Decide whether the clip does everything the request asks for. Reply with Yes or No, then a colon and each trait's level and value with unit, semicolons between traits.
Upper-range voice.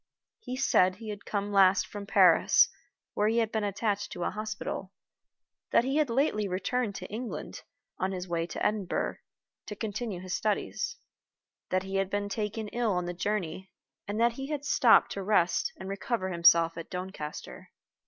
Yes: high, 205 Hz